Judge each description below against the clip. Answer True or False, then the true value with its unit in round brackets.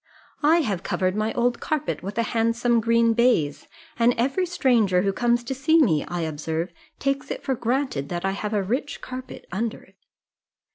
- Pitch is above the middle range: True (230 Hz)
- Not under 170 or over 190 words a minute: True (185 wpm)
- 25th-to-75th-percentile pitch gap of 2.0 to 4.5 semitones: False (5.0 semitones)